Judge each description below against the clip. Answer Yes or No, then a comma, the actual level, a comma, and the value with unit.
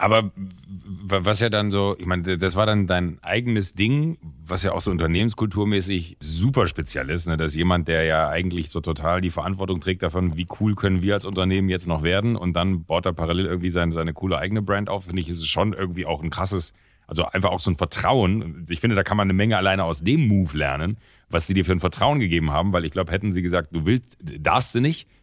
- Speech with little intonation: No, average, 3.0 semitones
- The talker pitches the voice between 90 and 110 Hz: Yes, very low, 95 Hz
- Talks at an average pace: No, fast, 235 wpm